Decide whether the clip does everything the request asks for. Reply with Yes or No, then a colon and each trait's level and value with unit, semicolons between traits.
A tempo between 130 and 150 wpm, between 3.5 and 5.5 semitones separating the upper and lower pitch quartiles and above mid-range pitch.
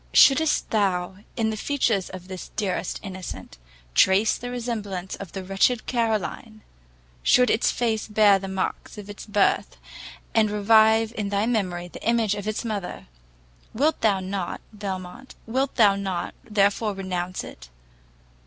No: average, 145 wpm; average, 2.8 semitones; high, 205 Hz